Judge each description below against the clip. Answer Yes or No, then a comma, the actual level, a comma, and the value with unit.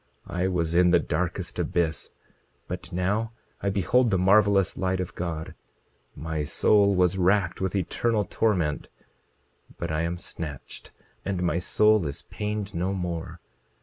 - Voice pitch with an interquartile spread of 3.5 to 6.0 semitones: No, average, 2.8 semitones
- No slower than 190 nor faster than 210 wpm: No, average, 145 wpm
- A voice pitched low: Yes, very low, 90 Hz